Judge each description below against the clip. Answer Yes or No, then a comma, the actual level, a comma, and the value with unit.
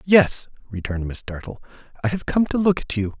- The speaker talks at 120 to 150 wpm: No, fast, 205 wpm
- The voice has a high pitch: No, low, 135 Hz